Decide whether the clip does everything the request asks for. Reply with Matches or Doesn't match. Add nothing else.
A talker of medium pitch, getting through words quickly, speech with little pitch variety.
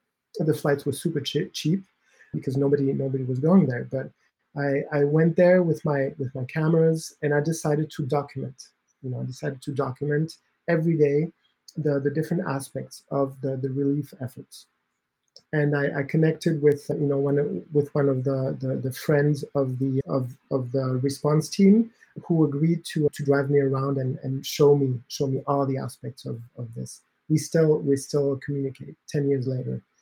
Doesn't match